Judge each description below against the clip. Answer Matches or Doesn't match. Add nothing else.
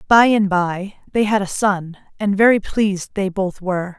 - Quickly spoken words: Doesn't match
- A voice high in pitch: Matches